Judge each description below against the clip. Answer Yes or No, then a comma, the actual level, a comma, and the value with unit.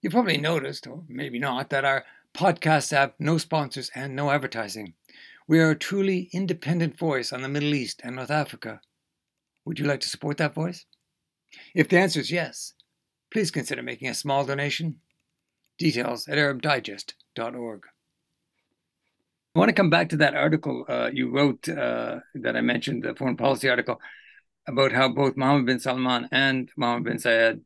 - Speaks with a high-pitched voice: No, medium, 140 Hz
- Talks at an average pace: Yes, average, 170 wpm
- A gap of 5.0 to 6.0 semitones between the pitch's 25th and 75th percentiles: No, average, 3.7 semitones